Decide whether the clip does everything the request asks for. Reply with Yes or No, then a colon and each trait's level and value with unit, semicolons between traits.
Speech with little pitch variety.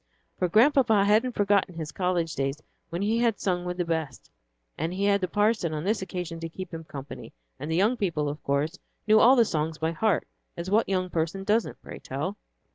No: average, 4.2 semitones